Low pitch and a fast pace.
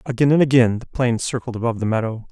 Yes: low, 120 Hz; fast, 235 wpm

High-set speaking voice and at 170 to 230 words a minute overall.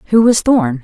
Yes: high, 195 Hz; fast, 215 wpm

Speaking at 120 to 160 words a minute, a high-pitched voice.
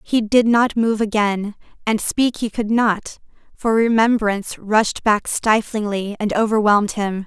Yes: average, 150 wpm; high, 215 Hz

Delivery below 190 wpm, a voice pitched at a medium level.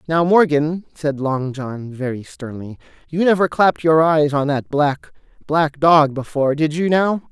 Yes: average, 165 wpm; medium, 150 Hz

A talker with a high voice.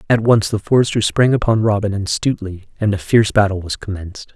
No: low, 105 Hz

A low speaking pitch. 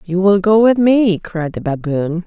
No: high, 190 Hz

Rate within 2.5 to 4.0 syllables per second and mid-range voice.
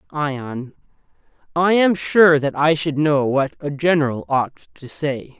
Yes: 3.7 syllables/s; medium, 150 Hz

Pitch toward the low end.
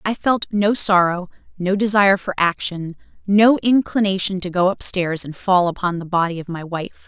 No: high, 190 Hz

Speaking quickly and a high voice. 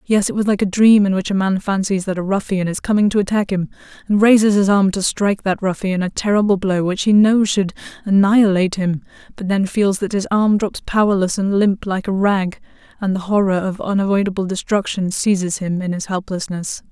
Yes: fast, 215 wpm; high, 195 Hz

